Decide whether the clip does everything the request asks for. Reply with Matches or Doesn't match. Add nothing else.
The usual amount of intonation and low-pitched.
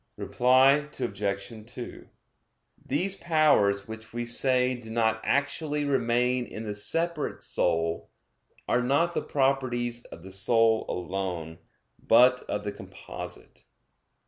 Matches